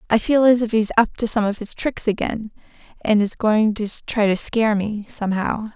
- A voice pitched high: Yes, high, 215 Hz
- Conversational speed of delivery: No, fast, 230 wpm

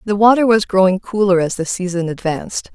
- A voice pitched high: Yes, high, 195 Hz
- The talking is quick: No, average, 195 wpm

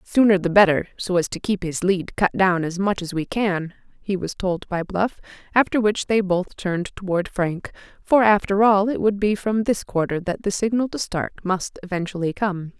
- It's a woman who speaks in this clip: Yes, female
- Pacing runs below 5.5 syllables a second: Yes, 5.0 syllables/s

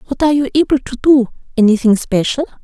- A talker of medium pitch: No, very high, 255 Hz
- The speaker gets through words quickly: No, average, 180 wpm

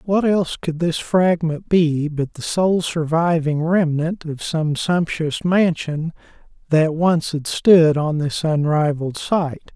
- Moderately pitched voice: Yes, medium, 160 Hz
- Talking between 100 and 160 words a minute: Yes, average, 140 wpm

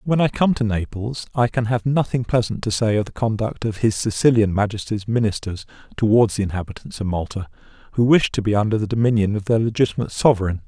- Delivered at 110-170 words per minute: No, average, 200 wpm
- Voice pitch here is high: No, low, 110 Hz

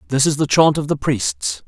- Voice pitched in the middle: No, low, 125 Hz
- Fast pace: Yes, fast, 250 wpm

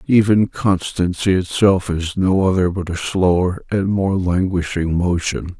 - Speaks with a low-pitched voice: Yes, very low, 90 Hz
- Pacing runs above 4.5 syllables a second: No, 4.1 syllables/s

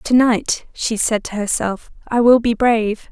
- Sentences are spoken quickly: No, average, 190 wpm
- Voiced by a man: No, female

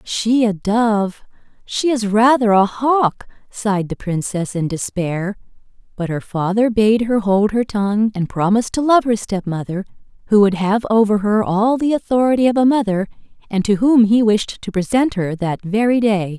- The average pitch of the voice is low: No, high, 215 Hz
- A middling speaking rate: Yes, average, 175 wpm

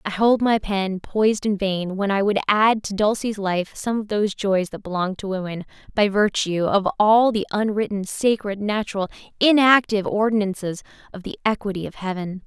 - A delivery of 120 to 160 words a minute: No, average, 180 wpm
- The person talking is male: No, female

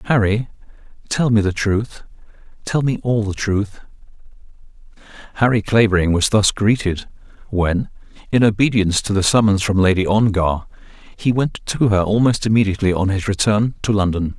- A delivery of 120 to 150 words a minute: Yes, average, 140 wpm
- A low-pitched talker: Yes, low, 105 Hz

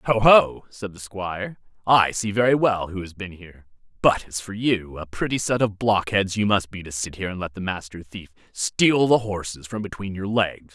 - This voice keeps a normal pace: No, fast, 225 wpm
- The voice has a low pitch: Yes, low, 100 Hz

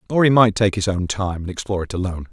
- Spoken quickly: Yes, fast, 285 wpm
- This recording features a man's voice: Yes, male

